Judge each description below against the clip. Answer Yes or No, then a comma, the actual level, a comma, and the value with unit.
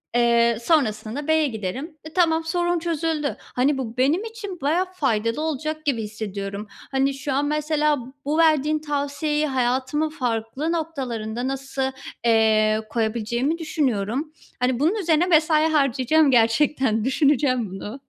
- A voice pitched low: No, very high, 280 Hz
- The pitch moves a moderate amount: Yes, average, 4.9 semitones